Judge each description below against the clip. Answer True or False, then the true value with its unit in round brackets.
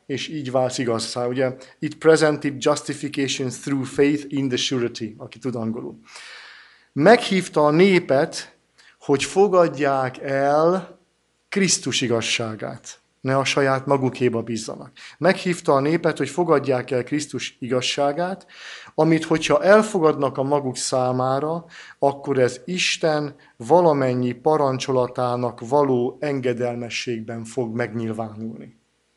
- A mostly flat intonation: False (3.6 semitones)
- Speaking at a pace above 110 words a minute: False (105 wpm)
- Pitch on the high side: False (135 Hz)